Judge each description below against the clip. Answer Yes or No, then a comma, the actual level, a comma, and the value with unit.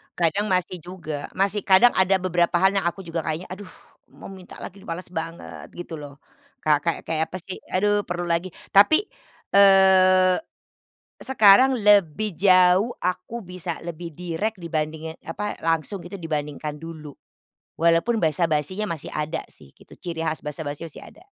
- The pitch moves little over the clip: No, average, 3.1 semitones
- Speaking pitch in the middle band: Yes, medium, 175 Hz